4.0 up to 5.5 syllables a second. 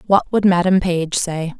Yes: 4.4 syllables/s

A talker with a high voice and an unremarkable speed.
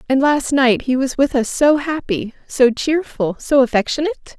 Yes: very high, 265 Hz; average, 180 wpm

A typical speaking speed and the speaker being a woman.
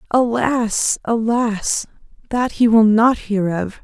No: slow, 125 wpm; female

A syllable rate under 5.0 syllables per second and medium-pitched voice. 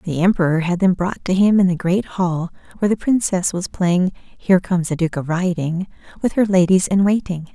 No: 5.4 syllables/s; medium, 180 Hz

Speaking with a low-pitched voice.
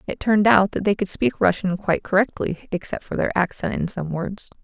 No: high, 190 Hz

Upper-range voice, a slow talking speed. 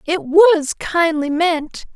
Yes: very high, 320 Hz; slow, 125 wpm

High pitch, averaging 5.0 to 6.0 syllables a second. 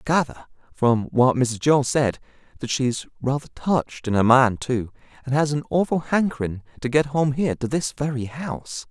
No: low, 130 Hz; 5.1 syllables/s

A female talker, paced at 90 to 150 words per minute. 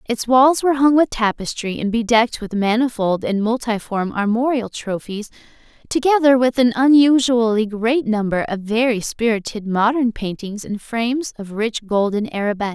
Yes: female; average, 145 wpm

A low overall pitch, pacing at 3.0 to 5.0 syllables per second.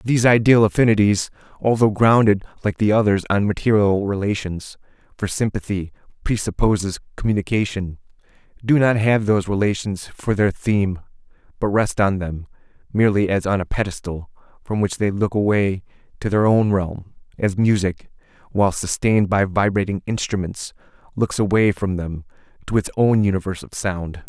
No: low, 100 Hz; 5.2 syllables/s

